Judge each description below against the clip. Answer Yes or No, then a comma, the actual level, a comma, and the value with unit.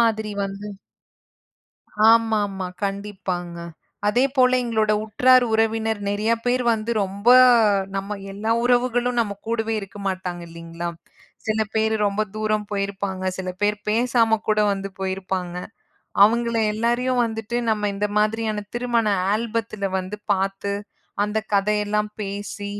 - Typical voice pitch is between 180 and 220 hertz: Yes, high, 210 Hz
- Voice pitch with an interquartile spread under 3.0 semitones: Yes, narrow, 2.4 semitones